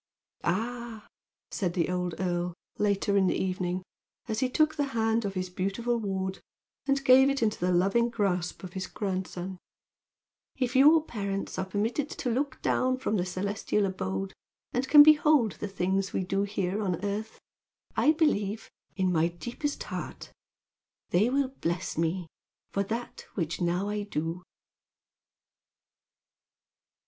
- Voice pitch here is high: Yes, high, 200 Hz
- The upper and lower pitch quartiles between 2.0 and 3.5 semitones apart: No, average, 4.7 semitones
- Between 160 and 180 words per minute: No, average, 145 wpm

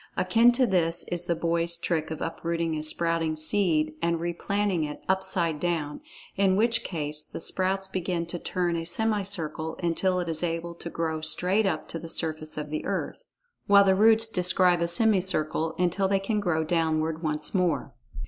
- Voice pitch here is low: No, medium, 170 Hz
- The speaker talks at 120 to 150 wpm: No, average, 175 wpm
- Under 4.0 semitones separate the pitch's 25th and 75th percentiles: Yes, average, 2.9 semitones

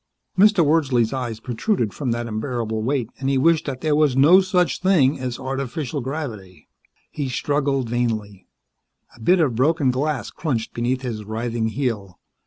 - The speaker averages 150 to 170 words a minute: Yes, average, 160 wpm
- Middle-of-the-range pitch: No, low, 130 Hz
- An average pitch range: Yes, average, 4.3 semitones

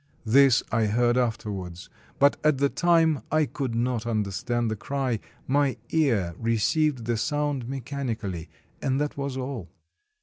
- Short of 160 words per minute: Yes, average, 140 wpm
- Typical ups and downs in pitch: Yes, average, 3.9 semitones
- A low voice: Yes, low, 125 Hz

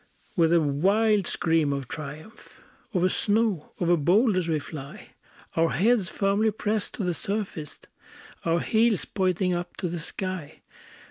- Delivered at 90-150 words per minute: Yes, average, 140 wpm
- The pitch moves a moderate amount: Yes, average, 4.1 semitones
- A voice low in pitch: No, medium, 180 Hz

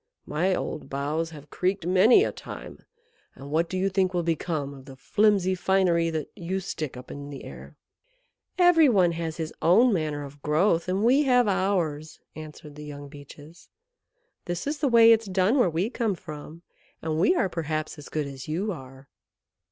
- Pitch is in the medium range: Yes, medium, 170 Hz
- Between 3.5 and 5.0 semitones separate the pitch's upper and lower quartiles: Yes, average, 4.4 semitones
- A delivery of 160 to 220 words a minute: Yes, average, 185 wpm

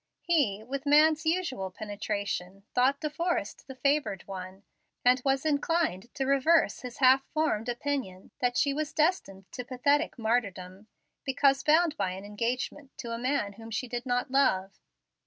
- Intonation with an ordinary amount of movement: No, wide, 5.7 semitones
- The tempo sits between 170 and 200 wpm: No, average, 155 wpm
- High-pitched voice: Yes, very high, 255 Hz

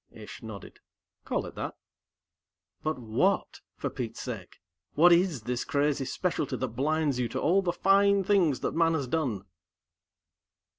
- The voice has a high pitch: No, medium, 145 Hz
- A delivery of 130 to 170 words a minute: Yes, average, 150 wpm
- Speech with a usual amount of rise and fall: No, wide, 5.7 semitones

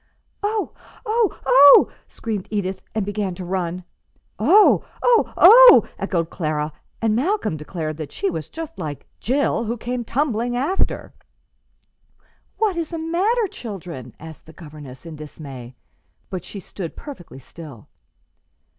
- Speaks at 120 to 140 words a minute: Yes, slow, 135 wpm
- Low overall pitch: No, high, 200 Hz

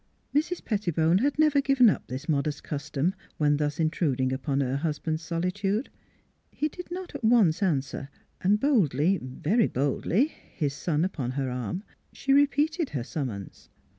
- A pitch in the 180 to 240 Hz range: No, medium, 165 Hz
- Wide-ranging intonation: Yes, wide, 8.8 semitones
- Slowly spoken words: No, average, 150 wpm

